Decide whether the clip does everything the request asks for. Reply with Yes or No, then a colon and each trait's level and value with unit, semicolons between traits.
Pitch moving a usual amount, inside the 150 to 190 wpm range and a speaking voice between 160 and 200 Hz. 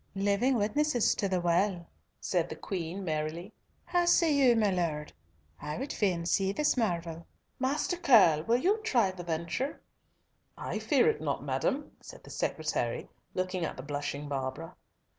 No: wide, 7.4 semitones; average, 160 wpm; high, 190 Hz